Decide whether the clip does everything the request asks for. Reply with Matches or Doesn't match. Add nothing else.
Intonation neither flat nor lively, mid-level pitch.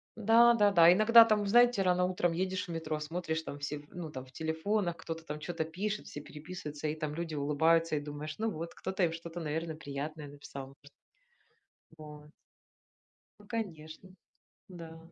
Matches